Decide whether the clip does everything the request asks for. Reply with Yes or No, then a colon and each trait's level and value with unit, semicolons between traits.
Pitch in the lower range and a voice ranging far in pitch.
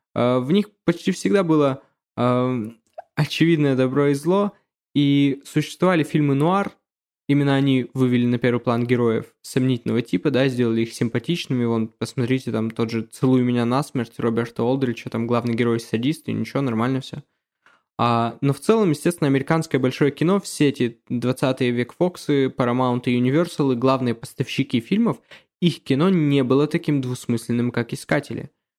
No: low, 130 Hz; average, 3.6 semitones